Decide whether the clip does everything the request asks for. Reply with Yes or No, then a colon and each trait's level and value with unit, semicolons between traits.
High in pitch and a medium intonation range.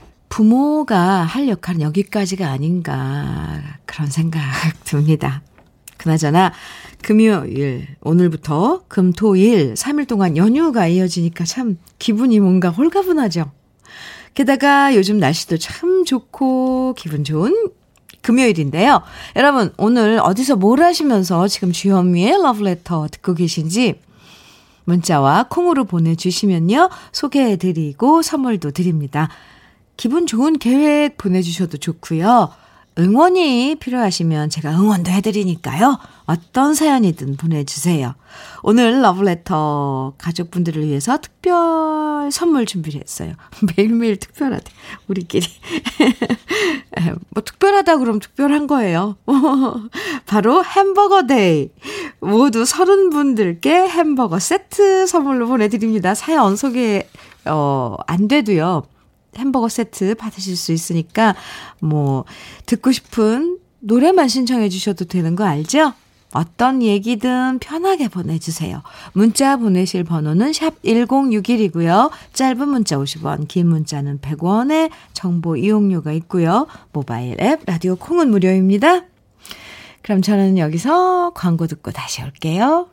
No: high, 205 Hz; wide, 8.2 semitones